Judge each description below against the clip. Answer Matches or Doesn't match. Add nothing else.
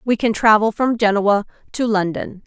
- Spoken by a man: Doesn't match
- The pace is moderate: Matches